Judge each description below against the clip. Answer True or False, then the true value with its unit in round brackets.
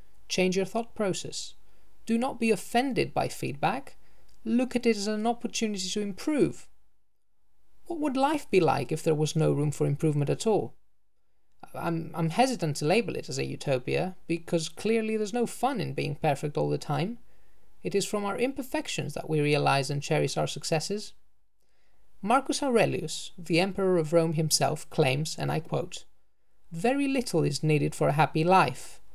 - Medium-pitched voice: True (180 Hz)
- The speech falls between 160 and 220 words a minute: True (170 wpm)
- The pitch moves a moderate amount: False (6.6 semitones)